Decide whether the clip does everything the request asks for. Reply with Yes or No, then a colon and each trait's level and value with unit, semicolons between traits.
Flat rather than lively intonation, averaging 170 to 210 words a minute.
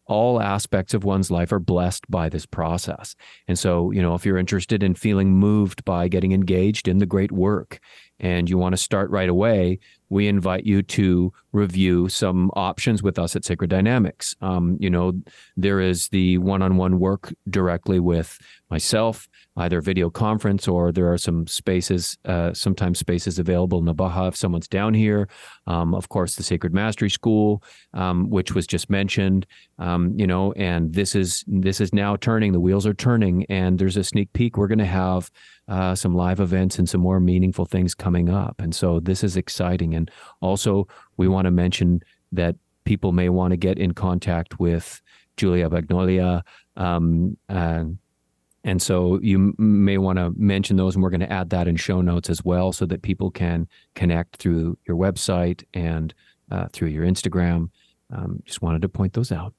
Yes: narrow, 1.9 semitones; average, 185 wpm